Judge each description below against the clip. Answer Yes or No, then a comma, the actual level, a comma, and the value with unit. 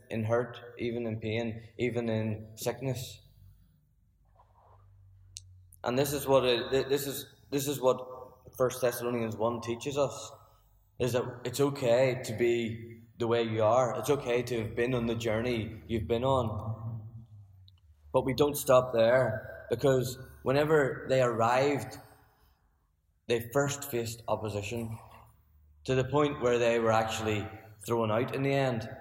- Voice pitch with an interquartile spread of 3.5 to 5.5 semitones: No, average, 2.9 semitones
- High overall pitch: No, low, 115 Hz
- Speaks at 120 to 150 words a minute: Yes, average, 145 wpm